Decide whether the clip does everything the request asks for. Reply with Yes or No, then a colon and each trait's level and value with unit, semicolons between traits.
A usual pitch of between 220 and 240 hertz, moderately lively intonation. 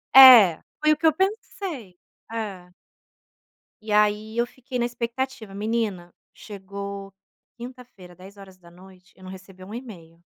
No: high, 210 Hz; average, 4.4 semitones